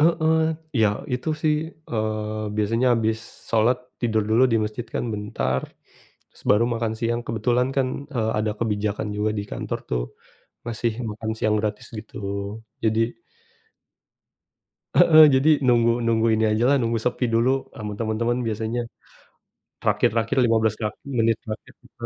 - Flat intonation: Yes, narrow, 1.9 semitones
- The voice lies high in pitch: No, low, 115 Hz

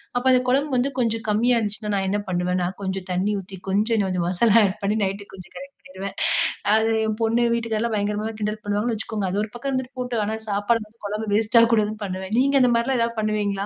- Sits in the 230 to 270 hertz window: No, high, 215 Hz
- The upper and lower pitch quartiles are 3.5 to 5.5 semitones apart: No, average, 2.8 semitones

